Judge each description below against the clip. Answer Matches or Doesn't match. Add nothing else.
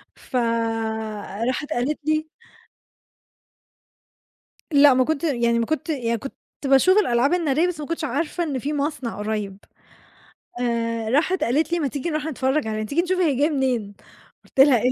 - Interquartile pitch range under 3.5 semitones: Doesn't match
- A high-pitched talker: Matches